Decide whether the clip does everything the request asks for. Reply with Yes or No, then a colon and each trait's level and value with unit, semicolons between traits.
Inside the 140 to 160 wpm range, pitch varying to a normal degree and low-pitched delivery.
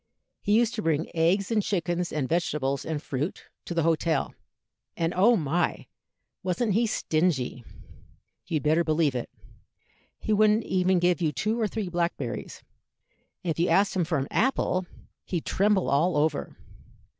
No: average, 155 wpm; average, 4.1 semitones; medium, 175 Hz